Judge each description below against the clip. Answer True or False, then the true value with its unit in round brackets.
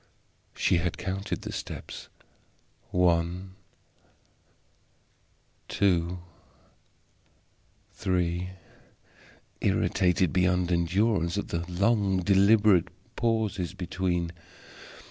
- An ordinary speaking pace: False (70 wpm)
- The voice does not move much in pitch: True (2.1 semitones)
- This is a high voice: False (90 Hz)